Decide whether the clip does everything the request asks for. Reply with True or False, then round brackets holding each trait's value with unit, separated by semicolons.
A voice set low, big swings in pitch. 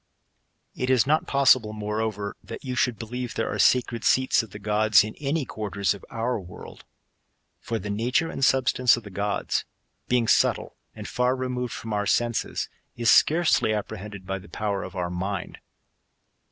False (110 Hz; 3.6 semitones)